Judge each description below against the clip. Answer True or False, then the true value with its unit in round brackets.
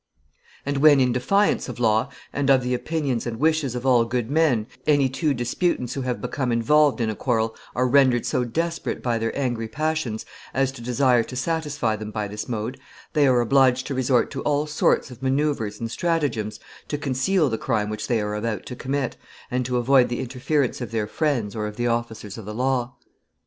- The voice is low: True (125 Hz)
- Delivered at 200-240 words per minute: True (205 wpm)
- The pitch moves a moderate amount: True (3.5 semitones)